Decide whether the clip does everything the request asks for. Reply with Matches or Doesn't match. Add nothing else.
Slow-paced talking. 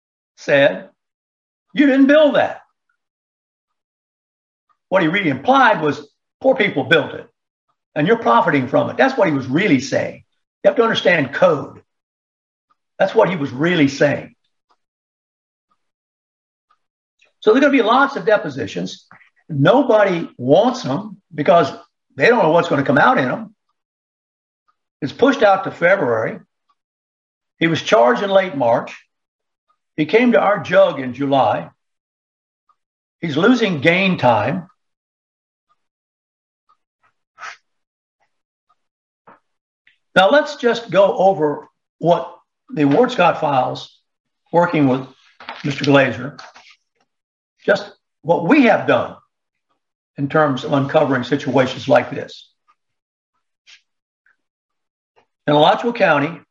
Matches